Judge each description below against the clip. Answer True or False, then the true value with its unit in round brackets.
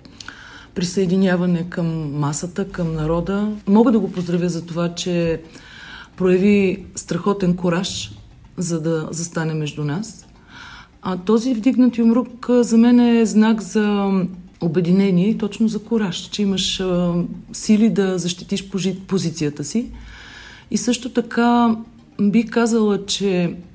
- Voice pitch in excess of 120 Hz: True (190 Hz)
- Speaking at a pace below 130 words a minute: True (120 wpm)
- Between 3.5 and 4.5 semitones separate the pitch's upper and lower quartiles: True (4.0 semitones)